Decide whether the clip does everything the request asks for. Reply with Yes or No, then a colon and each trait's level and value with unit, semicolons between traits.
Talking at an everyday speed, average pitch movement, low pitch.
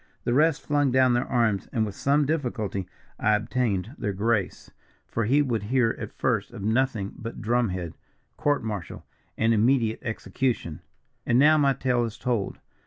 Yes: average, 170 wpm; average, 3.8 semitones; low, 120 Hz